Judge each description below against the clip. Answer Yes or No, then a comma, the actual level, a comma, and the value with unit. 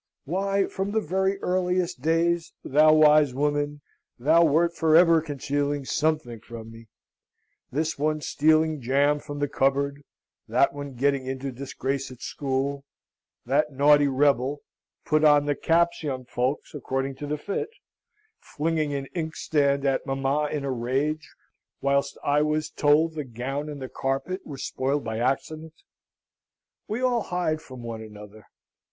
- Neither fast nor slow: Yes, average, 145 wpm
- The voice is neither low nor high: Yes, medium, 145 Hz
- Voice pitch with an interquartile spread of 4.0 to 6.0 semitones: No, narrow, 2.6 semitones